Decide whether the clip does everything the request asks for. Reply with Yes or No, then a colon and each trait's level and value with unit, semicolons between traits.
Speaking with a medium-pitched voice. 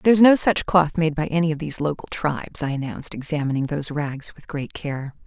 Yes: medium, 155 Hz